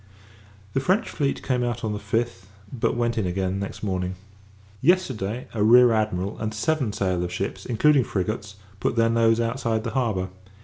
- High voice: No, low, 110 Hz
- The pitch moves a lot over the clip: No, average, 3.7 semitones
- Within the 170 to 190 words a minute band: Yes, average, 180 wpm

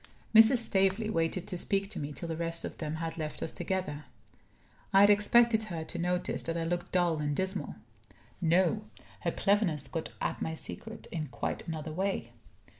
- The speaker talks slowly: No, average, 185 wpm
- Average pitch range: Yes, average, 3.6 semitones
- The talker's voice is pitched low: No, medium, 175 Hz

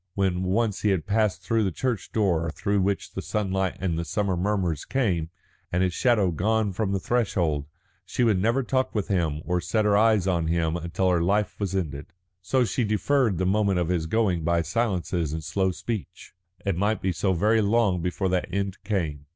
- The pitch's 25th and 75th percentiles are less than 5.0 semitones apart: Yes, average, 3.5 semitones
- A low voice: Yes, very low, 95 Hz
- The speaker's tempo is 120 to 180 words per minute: No, average, 200 wpm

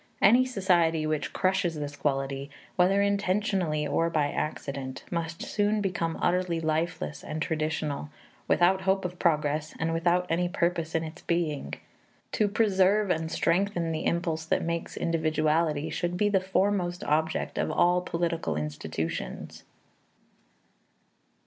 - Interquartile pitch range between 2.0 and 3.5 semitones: Yes, average, 3.0 semitones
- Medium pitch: Yes, medium, 170 Hz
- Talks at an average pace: No, slow, 130 wpm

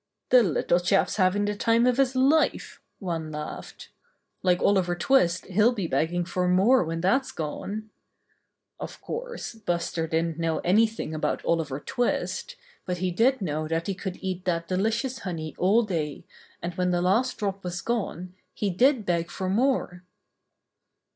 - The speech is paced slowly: No, average, 160 wpm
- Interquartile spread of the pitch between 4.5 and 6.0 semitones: Yes, average, 4.8 semitones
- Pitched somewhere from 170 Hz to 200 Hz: Yes, medium, 185 Hz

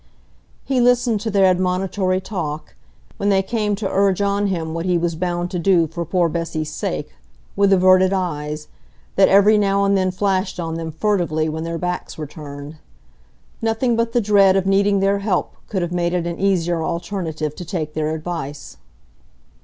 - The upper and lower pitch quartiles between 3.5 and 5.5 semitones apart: No, average, 3.1 semitones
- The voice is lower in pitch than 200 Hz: Yes, medium, 185 Hz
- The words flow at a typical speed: Yes, average, 180 wpm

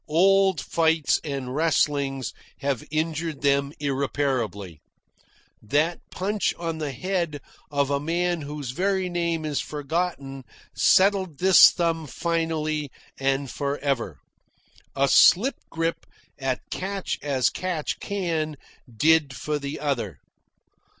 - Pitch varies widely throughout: No, average, 3.5 semitones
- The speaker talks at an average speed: No, slow, 115 wpm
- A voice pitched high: No, medium, 150 Hz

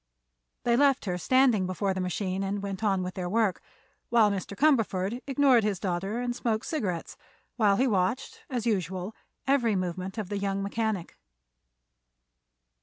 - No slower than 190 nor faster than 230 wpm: No, average, 155 wpm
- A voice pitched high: Yes, high, 205 Hz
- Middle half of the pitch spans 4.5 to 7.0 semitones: No, average, 4.1 semitones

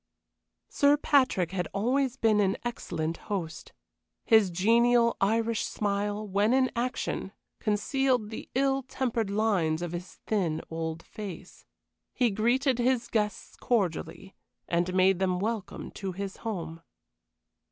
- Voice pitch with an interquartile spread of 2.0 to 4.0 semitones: No, average, 4.5 semitones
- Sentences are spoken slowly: Yes, slow, 125 wpm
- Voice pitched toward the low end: No, high, 210 Hz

